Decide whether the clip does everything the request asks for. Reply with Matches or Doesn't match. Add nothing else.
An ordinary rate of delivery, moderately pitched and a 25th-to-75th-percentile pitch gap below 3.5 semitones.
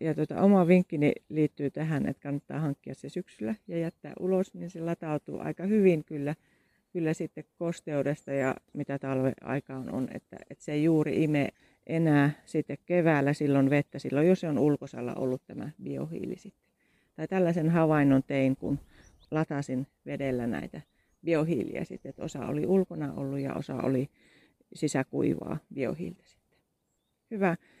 Matches